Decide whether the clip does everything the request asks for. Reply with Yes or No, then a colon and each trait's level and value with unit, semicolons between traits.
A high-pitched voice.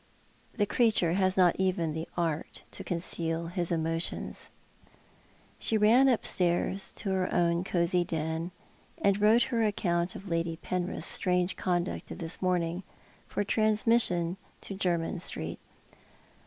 No: medium, 180 Hz